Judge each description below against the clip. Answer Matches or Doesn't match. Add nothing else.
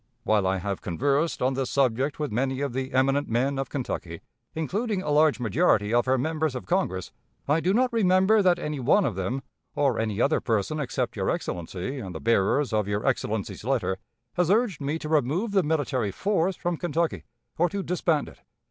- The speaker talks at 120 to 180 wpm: Doesn't match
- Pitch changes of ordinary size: Doesn't match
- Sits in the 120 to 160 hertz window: Matches